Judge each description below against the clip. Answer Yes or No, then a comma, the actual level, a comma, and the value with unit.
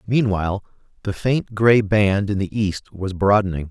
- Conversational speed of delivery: Yes, average, 160 wpm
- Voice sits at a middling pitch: No, low, 100 Hz